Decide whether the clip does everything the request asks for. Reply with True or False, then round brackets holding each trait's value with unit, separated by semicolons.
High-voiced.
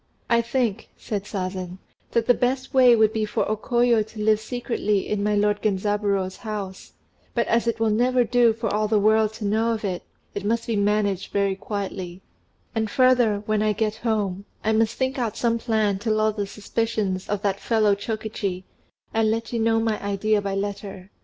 True (215 Hz)